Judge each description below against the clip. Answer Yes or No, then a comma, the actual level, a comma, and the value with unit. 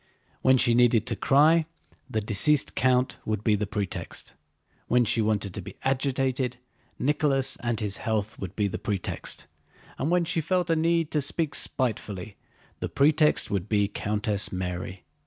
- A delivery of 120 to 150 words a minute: No, average, 160 wpm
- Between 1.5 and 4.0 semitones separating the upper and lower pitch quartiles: No, wide, 5.4 semitones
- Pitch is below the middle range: Yes, low, 120 Hz